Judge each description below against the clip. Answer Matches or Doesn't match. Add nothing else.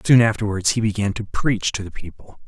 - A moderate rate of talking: Doesn't match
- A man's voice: Matches